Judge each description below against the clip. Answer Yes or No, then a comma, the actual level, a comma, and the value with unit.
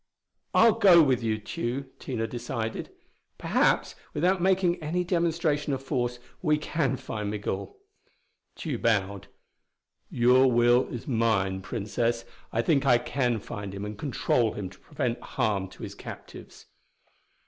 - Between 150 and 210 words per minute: No, slow, 135 wpm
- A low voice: Yes, low, 120 Hz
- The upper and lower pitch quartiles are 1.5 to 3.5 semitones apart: No, average, 5.1 semitones